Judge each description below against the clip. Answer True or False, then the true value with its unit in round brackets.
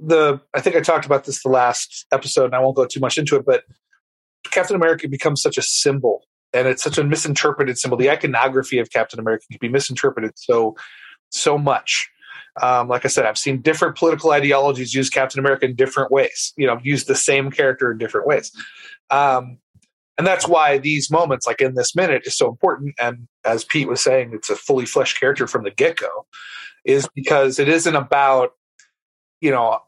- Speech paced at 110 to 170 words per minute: False (200 wpm)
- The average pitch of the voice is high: False (140 Hz)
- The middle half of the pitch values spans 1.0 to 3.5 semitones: False (4.1 semitones)